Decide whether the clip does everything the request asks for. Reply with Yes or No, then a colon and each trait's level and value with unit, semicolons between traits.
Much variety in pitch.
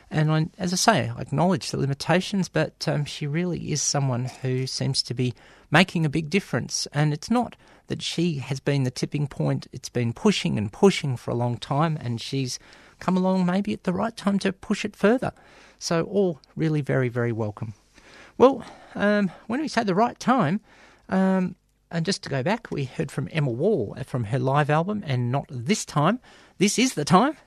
Yes: wide, 6.2 semitones